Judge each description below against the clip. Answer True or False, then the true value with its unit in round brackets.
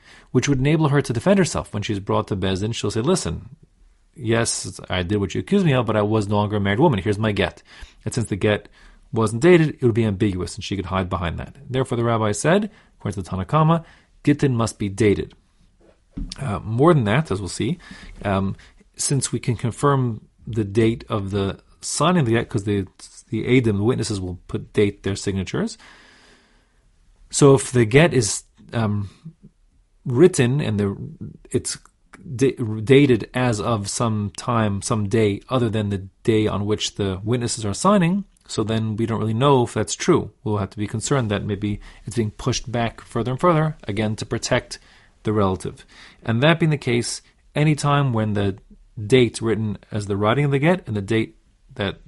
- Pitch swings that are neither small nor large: True (4.3 semitones)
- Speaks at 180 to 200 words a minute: True (195 wpm)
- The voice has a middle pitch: False (110 Hz)